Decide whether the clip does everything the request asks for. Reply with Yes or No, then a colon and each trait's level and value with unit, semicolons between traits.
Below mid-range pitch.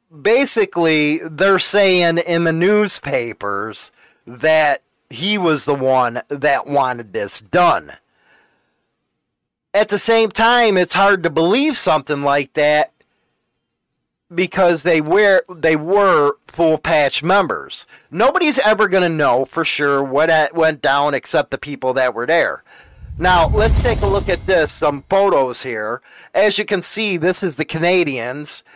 No: medium, 165 Hz